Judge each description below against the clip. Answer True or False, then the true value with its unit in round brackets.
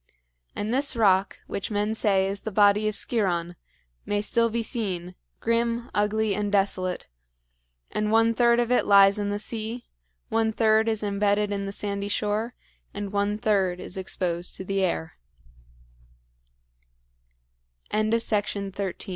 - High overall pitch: True (205 Hz)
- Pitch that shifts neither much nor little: False (2.0 semitones)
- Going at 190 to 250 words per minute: False (155 wpm)